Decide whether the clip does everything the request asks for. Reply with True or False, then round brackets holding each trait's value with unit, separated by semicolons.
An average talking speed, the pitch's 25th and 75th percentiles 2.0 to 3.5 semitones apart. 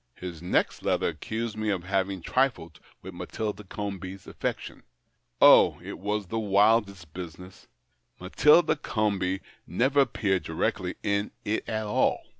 False (130 wpm; 2.8 semitones)